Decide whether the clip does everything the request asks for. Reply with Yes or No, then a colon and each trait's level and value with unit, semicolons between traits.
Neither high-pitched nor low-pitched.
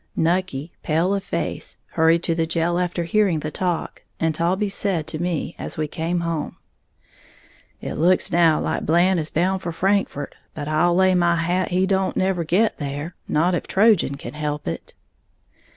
Yes: medium, 170 Hz